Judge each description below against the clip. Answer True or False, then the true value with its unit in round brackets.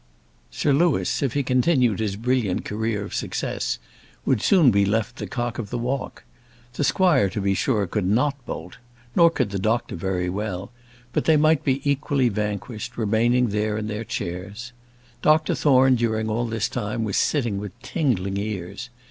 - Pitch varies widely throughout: False (4.3 semitones)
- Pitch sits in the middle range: False (115 Hz)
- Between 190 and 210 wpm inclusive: False (175 wpm)